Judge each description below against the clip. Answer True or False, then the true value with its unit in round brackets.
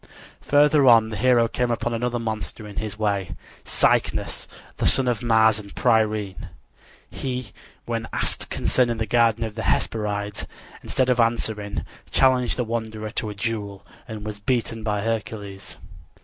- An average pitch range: False (2.2 semitones)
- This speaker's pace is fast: False (150 wpm)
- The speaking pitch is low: True (110 Hz)